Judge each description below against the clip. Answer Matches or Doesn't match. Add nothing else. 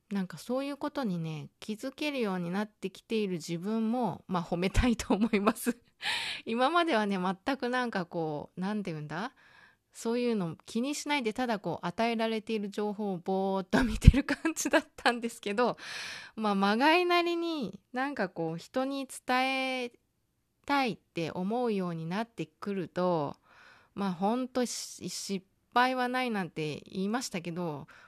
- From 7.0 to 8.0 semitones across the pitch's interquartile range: Doesn't match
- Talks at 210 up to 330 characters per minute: Matches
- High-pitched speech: Matches